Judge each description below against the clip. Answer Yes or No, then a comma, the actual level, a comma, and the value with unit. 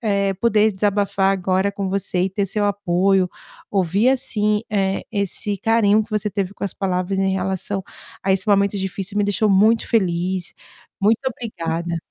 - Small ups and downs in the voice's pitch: Yes, narrow, 1.7 semitones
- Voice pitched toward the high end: Yes, high, 200 Hz